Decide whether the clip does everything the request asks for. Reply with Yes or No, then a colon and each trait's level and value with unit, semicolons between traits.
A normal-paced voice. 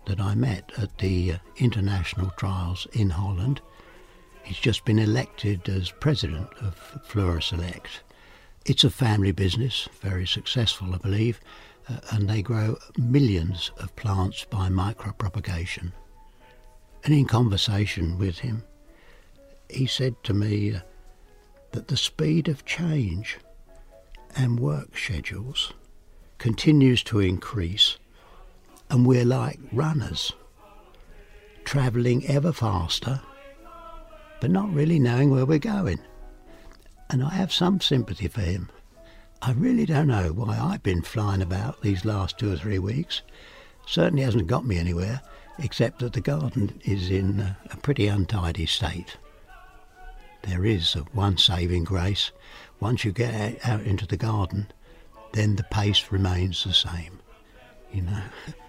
No: slow, 130 wpm